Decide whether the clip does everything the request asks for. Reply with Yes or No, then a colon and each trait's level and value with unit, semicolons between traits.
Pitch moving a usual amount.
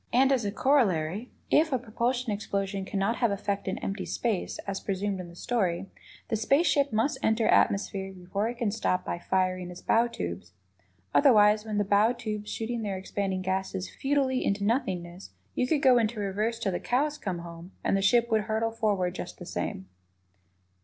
Yes: average, 3.7 semitones